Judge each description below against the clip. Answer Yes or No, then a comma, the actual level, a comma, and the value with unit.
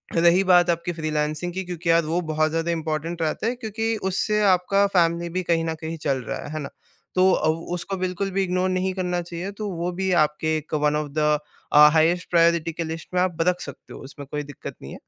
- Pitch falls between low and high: Yes, medium, 170 Hz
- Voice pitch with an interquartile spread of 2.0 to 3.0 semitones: Yes, narrow, 2.5 semitones